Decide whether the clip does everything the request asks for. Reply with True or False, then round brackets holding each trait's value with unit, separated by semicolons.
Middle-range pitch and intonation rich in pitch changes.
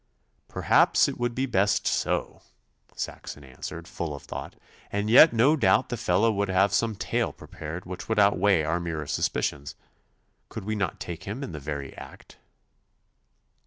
False (95 Hz; 5.7 semitones)